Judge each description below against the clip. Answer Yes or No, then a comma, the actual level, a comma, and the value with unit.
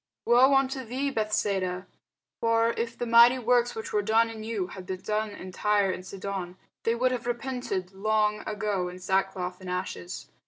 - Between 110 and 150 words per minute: No, average, 180 wpm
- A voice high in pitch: Yes, high, 215 Hz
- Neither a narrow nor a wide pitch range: Yes, average, 3.7 semitones